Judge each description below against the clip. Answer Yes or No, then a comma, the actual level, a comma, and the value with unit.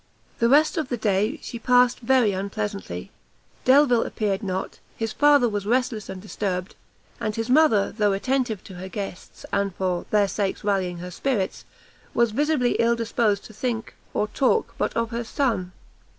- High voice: Yes, high, 220 Hz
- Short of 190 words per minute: Yes, average, 170 wpm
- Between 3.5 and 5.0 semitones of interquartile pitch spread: Yes, average, 3.9 semitones